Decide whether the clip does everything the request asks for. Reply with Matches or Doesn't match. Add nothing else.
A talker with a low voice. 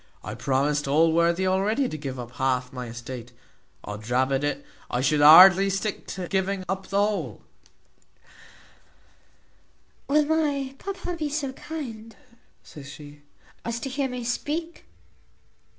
Doesn't match